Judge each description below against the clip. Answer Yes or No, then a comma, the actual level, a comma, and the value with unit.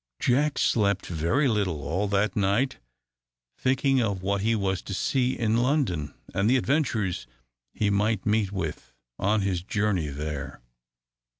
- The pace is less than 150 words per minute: Yes, average, 140 wpm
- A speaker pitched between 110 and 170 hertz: No, low, 100 Hz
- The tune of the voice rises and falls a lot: No, average, 4.3 semitones